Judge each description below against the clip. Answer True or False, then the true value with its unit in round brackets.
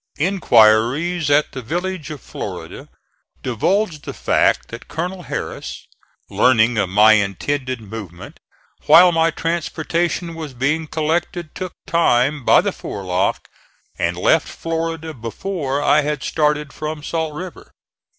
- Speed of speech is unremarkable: False (125 wpm)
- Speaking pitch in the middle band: True (150 Hz)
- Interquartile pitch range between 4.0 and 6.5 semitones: True (5.2 semitones)